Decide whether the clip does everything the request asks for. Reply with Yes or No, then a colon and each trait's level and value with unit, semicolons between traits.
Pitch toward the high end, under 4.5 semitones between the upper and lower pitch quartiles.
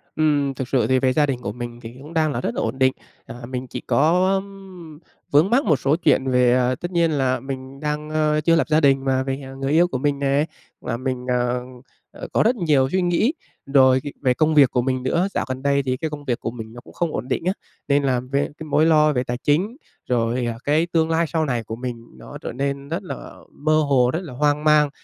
No: medium, 140 Hz; average, 3.4 semitones